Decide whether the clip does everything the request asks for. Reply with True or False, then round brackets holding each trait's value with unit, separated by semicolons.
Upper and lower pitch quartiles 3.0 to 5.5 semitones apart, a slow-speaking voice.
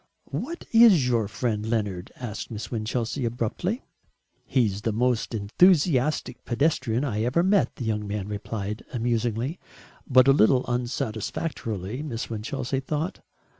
True (4.1 semitones; 130 wpm)